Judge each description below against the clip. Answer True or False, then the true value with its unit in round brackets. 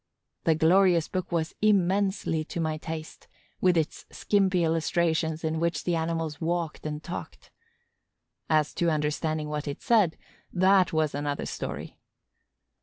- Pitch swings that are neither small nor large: False (2.2 semitones)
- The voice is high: False (165 Hz)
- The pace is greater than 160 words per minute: False (135 wpm)